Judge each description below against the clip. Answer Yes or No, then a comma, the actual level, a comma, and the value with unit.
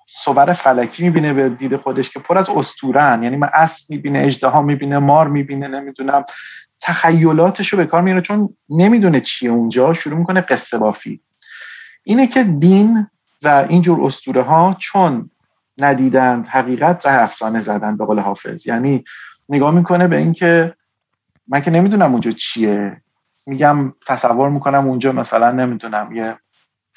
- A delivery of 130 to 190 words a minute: Yes, average, 145 wpm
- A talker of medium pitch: Yes, medium, 145 Hz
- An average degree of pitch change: Yes, average, 5.0 semitones